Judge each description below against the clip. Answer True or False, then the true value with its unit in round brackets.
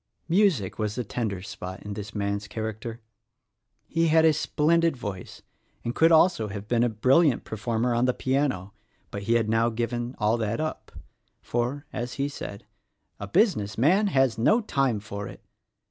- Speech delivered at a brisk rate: False (170 wpm)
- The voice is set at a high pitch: False (120 Hz)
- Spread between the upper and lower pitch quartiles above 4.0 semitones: True (5.4 semitones)